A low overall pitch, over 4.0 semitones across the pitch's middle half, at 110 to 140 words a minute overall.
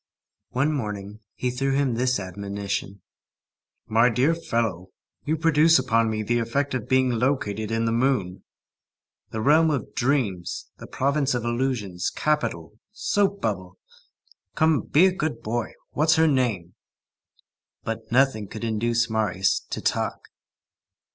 Yes: low, 120 Hz; average, 4.9 semitones; slow, 135 wpm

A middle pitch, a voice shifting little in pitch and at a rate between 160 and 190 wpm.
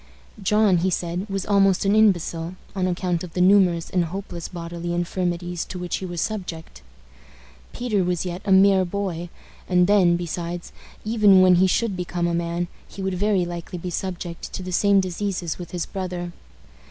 Yes: medium, 180 Hz; narrow, 2.0 semitones; average, 175 wpm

